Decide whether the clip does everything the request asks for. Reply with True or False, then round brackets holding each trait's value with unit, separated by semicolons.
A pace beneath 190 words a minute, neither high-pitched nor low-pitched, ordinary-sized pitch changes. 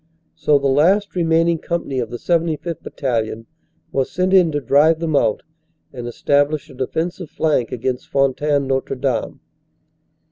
True (150 wpm; 145 Hz; 4.0 semitones)